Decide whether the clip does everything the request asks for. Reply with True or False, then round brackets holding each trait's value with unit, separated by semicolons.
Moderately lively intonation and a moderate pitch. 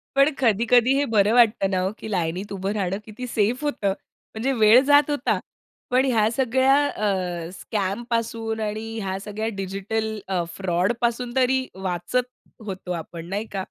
False (4.1 semitones; 215 Hz)